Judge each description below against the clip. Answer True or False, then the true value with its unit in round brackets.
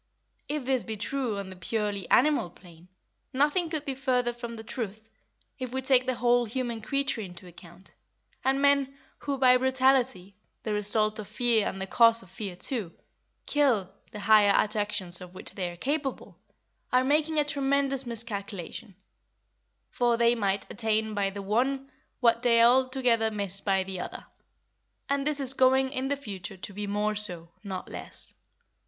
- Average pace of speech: True (170 wpm)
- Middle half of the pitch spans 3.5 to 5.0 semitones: True (4.7 semitones)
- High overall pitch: True (230 Hz)